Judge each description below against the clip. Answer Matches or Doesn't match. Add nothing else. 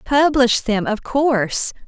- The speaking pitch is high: Matches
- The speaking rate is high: Doesn't match